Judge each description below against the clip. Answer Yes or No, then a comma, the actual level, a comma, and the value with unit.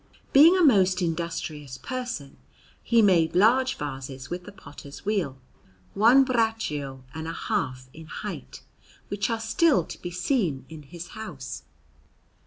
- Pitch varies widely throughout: Yes, wide, 7.5 semitones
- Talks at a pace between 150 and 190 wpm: No, average, 140 wpm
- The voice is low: No, medium, 175 Hz